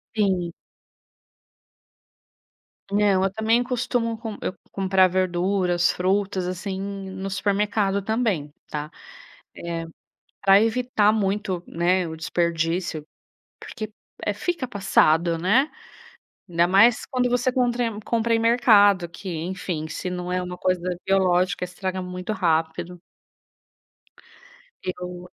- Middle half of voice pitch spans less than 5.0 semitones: Yes, average, 3.2 semitones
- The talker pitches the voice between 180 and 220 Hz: Yes, high, 190 Hz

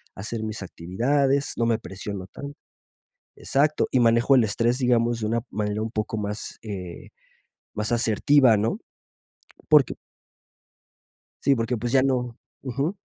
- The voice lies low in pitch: Yes, low, 115 Hz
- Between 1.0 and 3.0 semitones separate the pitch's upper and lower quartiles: No, average, 3.6 semitones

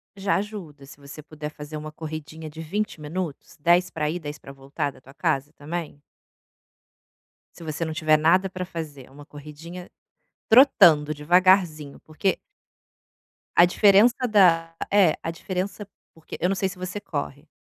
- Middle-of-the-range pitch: Yes, medium, 160 Hz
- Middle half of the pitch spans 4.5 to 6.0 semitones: No, average, 3.6 semitones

